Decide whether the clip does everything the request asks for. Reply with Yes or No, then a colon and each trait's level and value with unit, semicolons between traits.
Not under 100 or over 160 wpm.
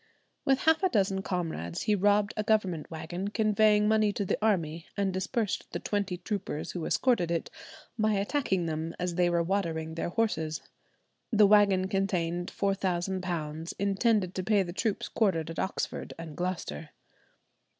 Yes: average, 155 wpm